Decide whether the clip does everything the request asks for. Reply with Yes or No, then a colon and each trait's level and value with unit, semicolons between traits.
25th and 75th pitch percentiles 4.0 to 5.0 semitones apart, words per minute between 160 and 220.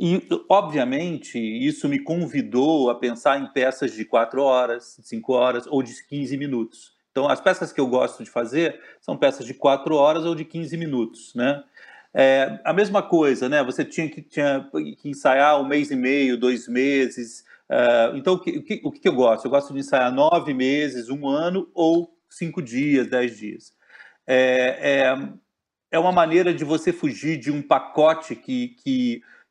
Yes: average, 4.6 semitones; average, 180 wpm